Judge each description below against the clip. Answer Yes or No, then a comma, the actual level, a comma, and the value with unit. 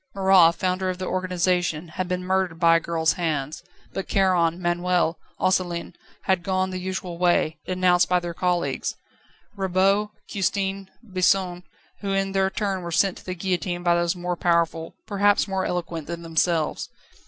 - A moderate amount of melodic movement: No, narrow, 1.8 semitones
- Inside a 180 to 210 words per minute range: No, average, 160 wpm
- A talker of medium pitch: Yes, medium, 180 Hz